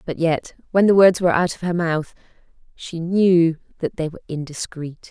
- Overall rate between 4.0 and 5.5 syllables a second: Yes, 5.0 syllables/s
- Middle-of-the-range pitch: Yes, medium, 170 Hz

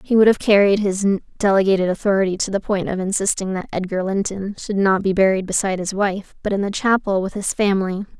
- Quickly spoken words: Yes, fast, 210 wpm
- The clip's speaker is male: No, female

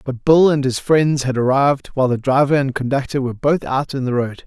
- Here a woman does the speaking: No, male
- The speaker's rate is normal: No, fast, 240 wpm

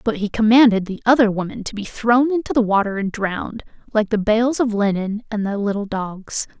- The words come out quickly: Yes, fast, 210 wpm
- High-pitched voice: Yes, high, 215 Hz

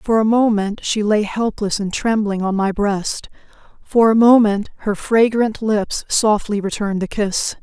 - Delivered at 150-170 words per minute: Yes, average, 165 wpm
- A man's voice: No, female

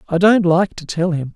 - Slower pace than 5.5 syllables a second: Yes, 5.0 syllables/s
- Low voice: No, medium, 175 Hz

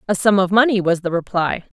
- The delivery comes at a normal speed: No, fast, 235 wpm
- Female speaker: Yes, female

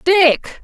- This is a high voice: Yes, very high, 340 Hz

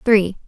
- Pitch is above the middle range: Yes, high, 200 Hz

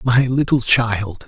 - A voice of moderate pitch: No, low, 120 Hz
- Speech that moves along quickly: No, average, 140 wpm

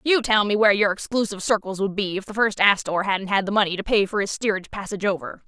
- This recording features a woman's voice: Yes, female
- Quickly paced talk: Yes, fast, 265 wpm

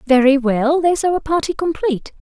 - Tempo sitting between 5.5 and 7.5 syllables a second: Yes, 5.8 syllables/s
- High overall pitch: Yes, very high, 295 Hz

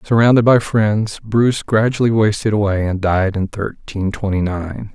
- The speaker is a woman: No, male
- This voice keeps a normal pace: Yes, average, 160 wpm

